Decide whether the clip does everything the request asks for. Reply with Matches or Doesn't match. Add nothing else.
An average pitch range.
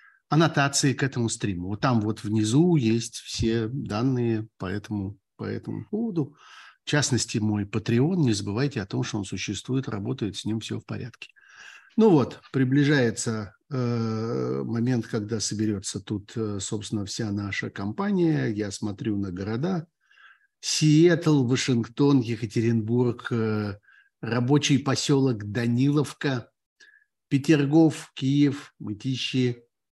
Matches